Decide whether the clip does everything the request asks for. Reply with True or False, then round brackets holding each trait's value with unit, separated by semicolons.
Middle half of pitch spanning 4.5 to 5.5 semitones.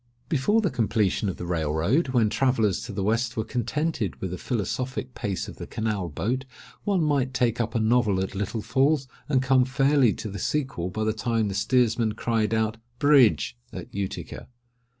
False (4.1 semitones)